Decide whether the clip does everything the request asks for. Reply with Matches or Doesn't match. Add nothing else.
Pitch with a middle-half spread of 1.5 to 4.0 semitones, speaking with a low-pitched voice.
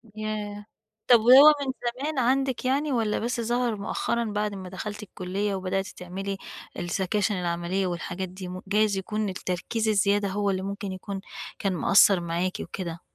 Doesn't match